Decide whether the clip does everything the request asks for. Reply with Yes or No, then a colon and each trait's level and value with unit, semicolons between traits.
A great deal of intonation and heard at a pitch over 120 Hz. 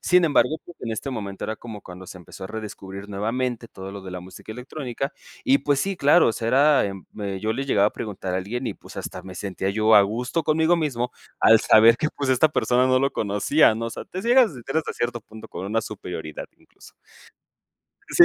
No: wide, 5.7 semitones; low, 115 Hz